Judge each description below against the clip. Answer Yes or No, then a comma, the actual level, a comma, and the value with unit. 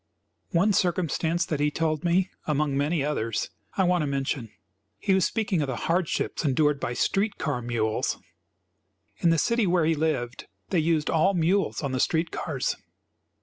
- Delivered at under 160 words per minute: No, average, 170 wpm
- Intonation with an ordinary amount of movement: Yes, average, 4.1 semitones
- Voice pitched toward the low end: No, medium, 160 Hz